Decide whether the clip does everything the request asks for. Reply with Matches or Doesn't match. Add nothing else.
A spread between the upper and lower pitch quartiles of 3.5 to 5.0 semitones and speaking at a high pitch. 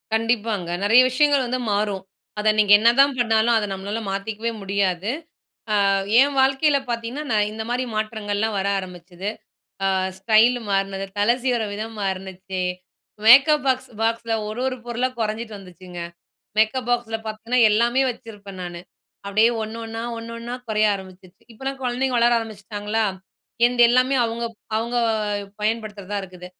Doesn't match